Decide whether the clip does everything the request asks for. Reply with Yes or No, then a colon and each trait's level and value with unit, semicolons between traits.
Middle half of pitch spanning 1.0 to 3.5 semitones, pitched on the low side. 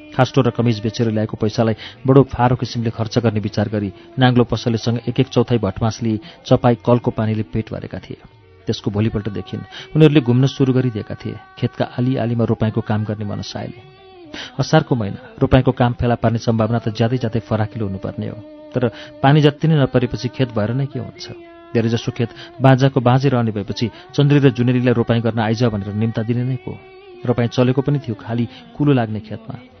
Yes: narrow, 2.6 semitones; low, 120 Hz